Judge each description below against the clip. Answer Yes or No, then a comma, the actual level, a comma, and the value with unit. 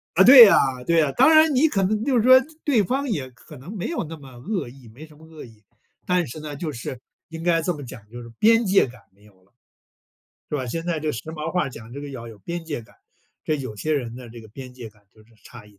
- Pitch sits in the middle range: Yes, medium, 150 Hz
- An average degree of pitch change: No, wide, 7.0 semitones